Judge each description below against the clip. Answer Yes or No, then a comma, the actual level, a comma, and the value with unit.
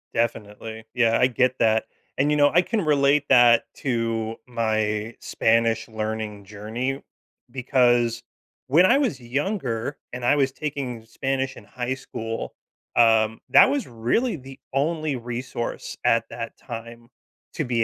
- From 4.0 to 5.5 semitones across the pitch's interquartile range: No, average, 3.2 semitones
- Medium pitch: No, low, 120 Hz